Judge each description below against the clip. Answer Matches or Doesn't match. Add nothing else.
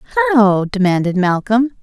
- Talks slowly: Matches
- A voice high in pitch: Matches